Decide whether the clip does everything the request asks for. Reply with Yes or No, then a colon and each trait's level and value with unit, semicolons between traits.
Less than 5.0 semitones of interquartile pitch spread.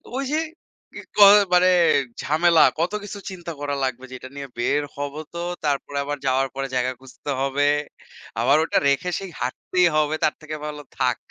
Yes: average, 3.9 semitones